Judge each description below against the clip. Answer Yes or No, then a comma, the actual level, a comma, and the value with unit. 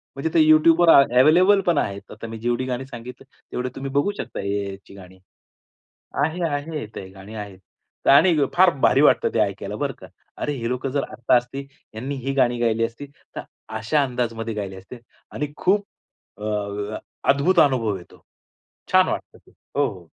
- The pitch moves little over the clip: No, average, 5.1 semitones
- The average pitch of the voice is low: Yes, low, 125 Hz